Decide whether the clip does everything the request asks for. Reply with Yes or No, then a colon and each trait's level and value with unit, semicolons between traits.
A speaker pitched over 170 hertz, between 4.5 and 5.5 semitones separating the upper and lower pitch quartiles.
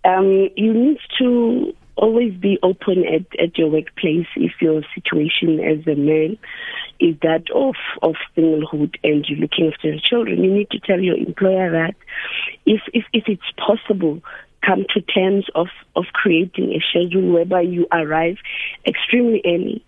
Yes: medium, 185 Hz; average, 5.0 semitones